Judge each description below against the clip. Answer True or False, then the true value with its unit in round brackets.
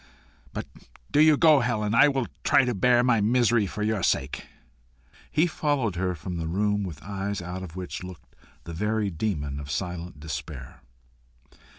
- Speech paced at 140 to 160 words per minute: False (170 wpm)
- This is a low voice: True (100 Hz)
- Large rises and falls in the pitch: True (5.7 semitones)